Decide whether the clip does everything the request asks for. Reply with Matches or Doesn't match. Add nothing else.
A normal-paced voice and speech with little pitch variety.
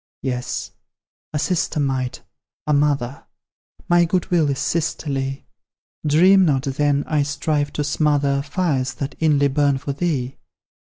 Doesn't match